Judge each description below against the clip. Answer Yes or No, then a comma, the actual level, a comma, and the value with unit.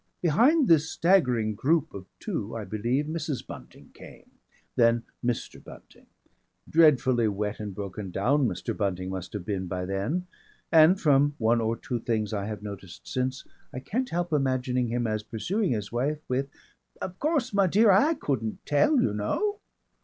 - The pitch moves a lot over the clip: Yes, wide, 7.4 semitones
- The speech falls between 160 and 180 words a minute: Yes, average, 165 wpm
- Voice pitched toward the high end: No, low, 125 Hz